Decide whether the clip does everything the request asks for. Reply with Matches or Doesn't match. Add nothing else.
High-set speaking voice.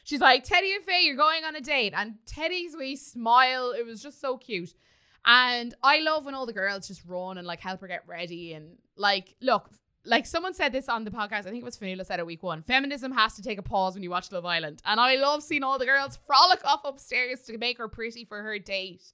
Matches